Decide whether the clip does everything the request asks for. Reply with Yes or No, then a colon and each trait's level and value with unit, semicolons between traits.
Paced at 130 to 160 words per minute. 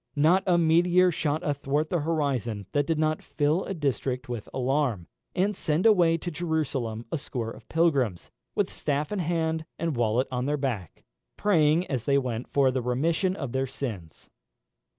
No: average, 170 wpm